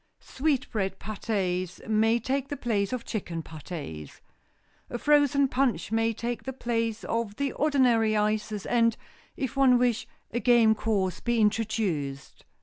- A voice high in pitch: Yes, high, 225 Hz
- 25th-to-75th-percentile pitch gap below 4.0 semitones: Yes, average, 3.3 semitones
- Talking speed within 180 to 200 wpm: No, average, 140 wpm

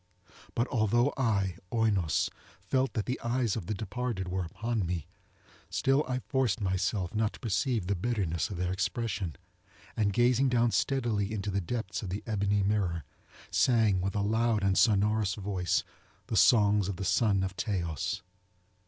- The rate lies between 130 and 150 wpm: No, average, 160 wpm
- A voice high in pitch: No, low, 105 Hz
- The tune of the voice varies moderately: Yes, average, 3.6 semitones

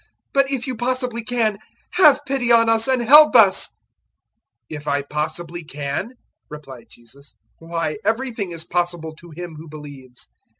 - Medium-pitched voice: Yes, medium, 175 Hz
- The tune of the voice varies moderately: No, wide, 8.1 semitones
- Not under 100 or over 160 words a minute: Yes, average, 155 wpm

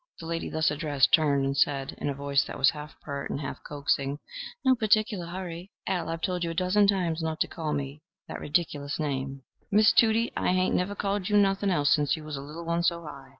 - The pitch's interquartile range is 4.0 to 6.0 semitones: Yes, average, 4.3 semitones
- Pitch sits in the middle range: Yes, medium, 160 Hz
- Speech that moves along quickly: Yes, fast, 230 wpm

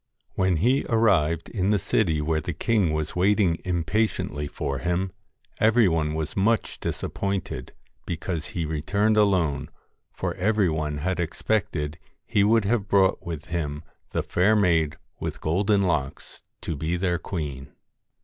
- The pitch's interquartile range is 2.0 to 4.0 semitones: No, average, 4.5 semitones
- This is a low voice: Yes, very low, 90 Hz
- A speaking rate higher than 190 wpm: No, average, 145 wpm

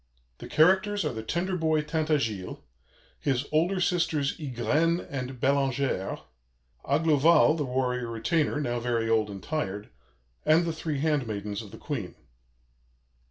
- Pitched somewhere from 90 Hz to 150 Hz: Yes, medium, 140 Hz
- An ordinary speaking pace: No, slow, 130 wpm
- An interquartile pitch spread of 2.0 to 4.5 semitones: No, average, 5.2 semitones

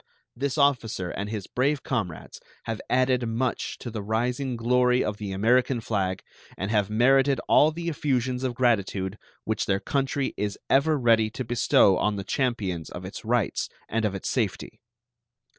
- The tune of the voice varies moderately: Yes, average, 3.8 semitones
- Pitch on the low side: Yes, low, 115 Hz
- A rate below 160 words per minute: No, average, 165 wpm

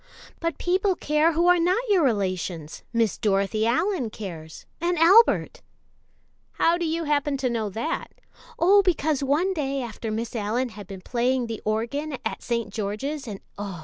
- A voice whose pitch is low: No, very high, 260 Hz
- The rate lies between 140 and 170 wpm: Yes, average, 165 wpm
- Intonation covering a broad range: Yes, wide, 7.5 semitones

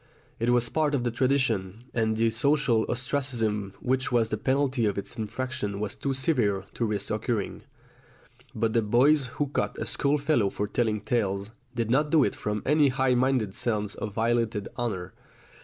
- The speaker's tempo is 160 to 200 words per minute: Yes, average, 175 wpm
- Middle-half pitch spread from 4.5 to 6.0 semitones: No, average, 3.8 semitones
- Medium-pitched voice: No, low, 115 Hz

